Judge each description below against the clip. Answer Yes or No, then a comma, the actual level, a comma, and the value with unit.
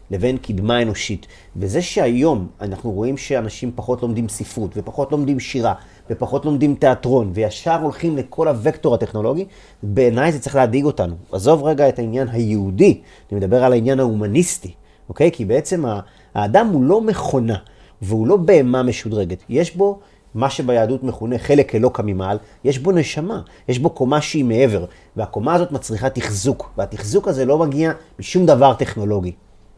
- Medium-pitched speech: No, low, 125 Hz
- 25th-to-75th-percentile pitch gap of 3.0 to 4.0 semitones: No, average, 5.2 semitones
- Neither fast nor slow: No, fast, 155 wpm